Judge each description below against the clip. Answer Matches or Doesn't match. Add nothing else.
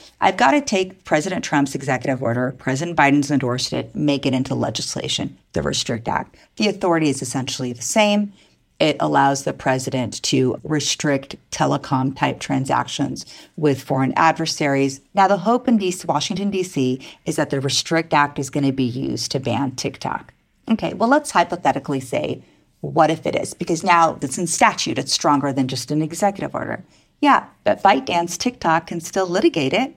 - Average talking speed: Matches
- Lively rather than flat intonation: Doesn't match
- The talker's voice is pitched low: Doesn't match